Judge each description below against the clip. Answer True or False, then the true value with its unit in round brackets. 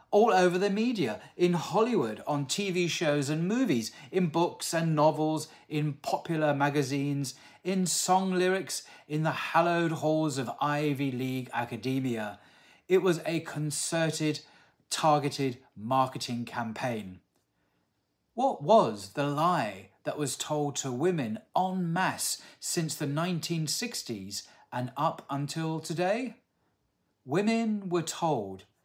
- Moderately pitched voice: True (155 Hz)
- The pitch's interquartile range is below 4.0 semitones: False (4.8 semitones)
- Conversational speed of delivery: False (120 wpm)